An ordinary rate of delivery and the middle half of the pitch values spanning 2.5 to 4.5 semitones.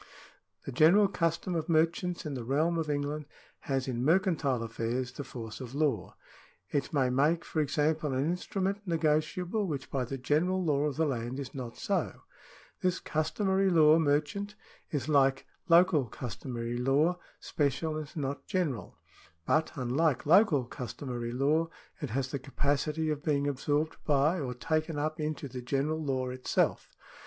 Yes: average, 155 wpm; average, 3.5 semitones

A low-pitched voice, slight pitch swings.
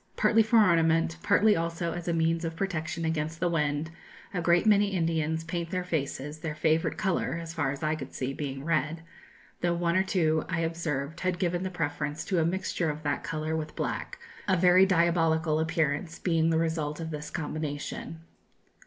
No: medium, 165 Hz; narrow, 1.9 semitones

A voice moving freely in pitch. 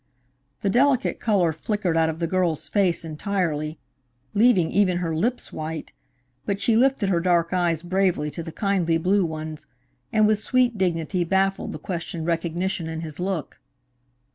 No: average, 3.5 semitones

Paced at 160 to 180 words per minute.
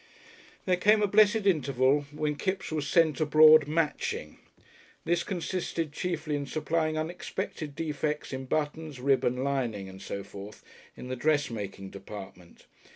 No: slow, 135 wpm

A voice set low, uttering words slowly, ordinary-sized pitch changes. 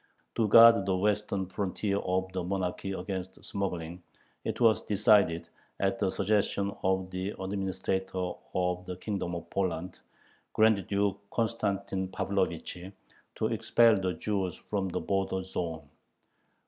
No: very low, 95 Hz; slow, 130 wpm; narrow, 1.6 semitones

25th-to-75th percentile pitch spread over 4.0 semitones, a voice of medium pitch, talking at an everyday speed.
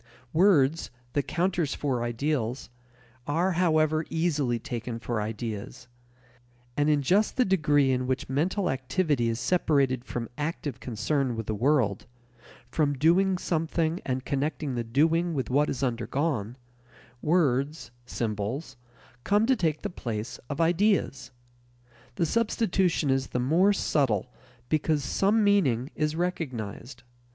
No: average, 5.1 semitones; medium, 145 Hz; slow, 130 wpm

